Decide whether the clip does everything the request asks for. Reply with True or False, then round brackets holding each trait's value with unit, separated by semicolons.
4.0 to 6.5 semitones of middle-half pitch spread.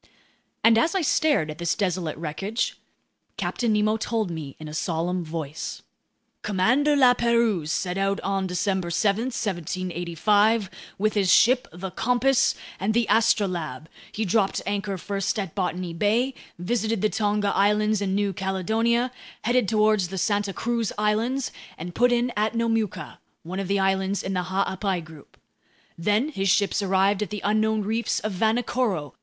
False (3.5 semitones)